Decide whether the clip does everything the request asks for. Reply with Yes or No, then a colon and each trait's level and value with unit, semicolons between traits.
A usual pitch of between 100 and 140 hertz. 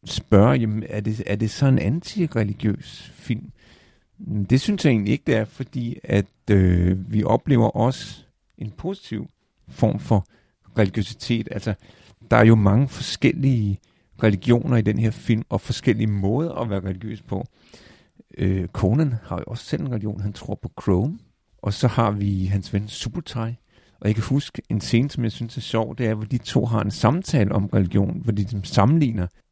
Yes: low, 110 Hz